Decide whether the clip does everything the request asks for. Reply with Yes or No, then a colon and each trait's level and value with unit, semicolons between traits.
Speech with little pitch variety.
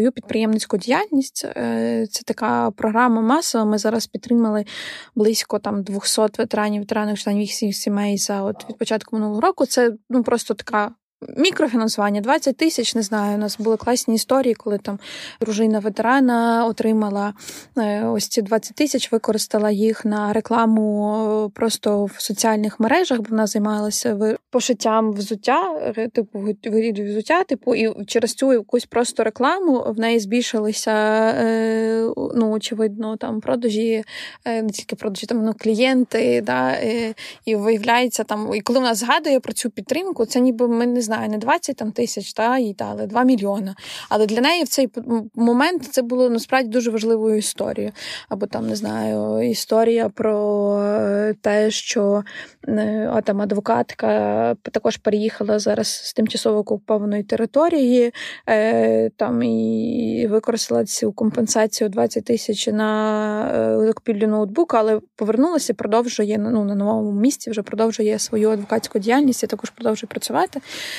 Yes: narrow, 2.1 semitones